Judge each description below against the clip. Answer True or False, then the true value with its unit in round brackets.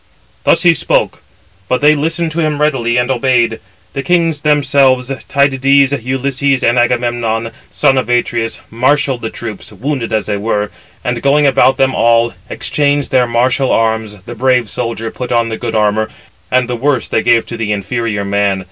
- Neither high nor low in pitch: False (125 Hz)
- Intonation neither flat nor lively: True (3.3 semitones)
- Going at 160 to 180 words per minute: True (175 wpm)